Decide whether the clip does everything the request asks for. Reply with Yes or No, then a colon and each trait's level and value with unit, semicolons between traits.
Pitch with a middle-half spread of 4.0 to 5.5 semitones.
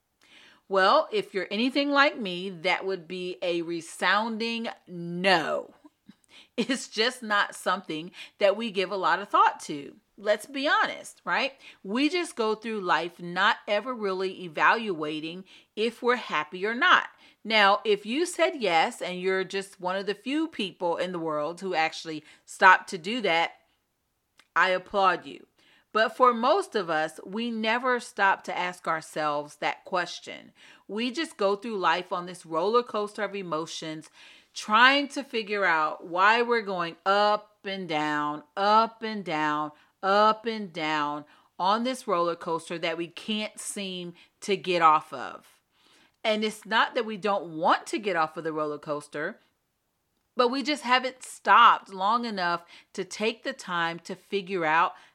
Yes: average, 4.7 semitones